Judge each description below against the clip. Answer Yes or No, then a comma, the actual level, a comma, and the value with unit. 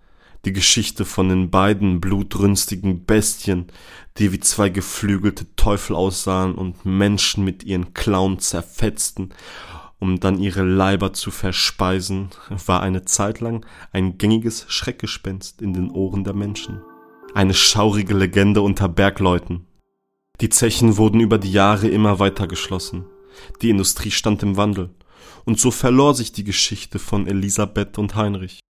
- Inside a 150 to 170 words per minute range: No, average, 140 wpm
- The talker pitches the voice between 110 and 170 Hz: No, low, 100 Hz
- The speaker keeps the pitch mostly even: Yes, narrow, 1.9 semitones